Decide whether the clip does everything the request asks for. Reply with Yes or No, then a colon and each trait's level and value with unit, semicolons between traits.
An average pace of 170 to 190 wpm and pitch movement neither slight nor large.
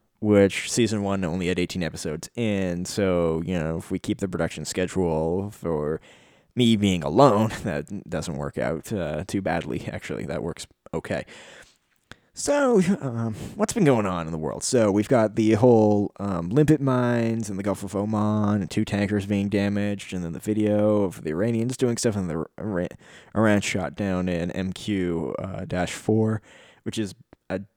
Yes: average, 175 wpm; average, 3.3 semitones